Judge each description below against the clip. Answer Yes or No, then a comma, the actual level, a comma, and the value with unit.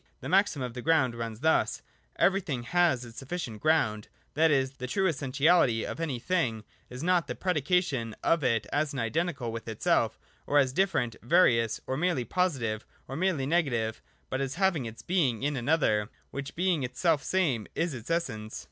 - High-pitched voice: No, medium, 140 Hz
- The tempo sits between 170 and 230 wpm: Yes, average, 175 wpm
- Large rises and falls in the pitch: Yes, wide, 6.1 semitones